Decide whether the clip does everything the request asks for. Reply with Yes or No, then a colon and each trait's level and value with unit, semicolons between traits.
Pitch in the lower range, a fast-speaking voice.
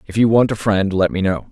Yes: low, 100 Hz; fast, 315 wpm